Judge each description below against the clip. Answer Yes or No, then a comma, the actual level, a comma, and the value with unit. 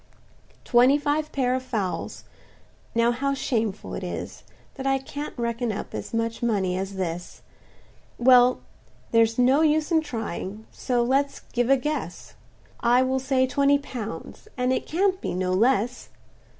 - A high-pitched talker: Yes, very high, 250 Hz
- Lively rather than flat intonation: No, average, 3.2 semitones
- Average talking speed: Yes, average, 150 wpm